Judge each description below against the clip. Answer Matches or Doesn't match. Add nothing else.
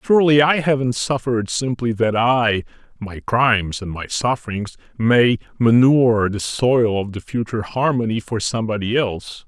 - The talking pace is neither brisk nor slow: Matches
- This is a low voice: Matches